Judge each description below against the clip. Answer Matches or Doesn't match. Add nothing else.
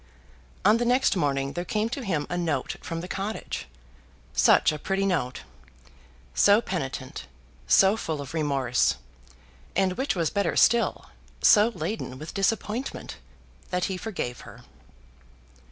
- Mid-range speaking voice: Matches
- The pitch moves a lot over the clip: Matches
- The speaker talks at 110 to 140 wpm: Matches